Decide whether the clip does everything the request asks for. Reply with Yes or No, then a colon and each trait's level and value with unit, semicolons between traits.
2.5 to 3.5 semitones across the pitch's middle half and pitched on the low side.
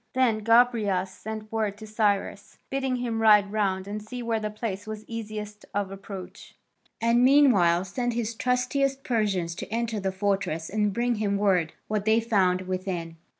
No: average, 3.0 semitones; high, 215 Hz